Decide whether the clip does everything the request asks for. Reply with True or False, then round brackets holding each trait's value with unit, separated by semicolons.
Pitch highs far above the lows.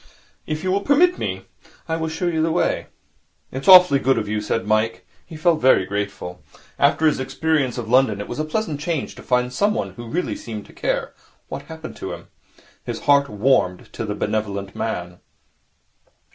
True (6.9 semitones)